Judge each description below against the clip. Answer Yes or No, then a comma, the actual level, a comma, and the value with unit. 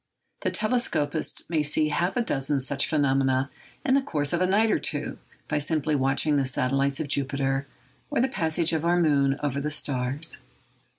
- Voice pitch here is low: No, medium, 145 Hz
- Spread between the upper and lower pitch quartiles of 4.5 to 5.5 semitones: No, average, 3.2 semitones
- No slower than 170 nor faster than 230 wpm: Yes, average, 180 wpm